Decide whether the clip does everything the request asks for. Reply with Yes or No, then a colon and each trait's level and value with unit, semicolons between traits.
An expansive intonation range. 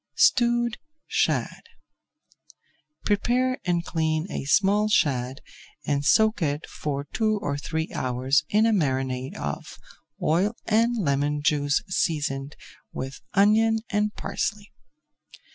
Yes: wide, 7.1 semitones